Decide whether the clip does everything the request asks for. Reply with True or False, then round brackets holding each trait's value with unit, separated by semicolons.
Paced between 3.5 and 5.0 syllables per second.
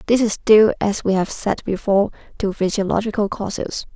False (5.4 syllables/s)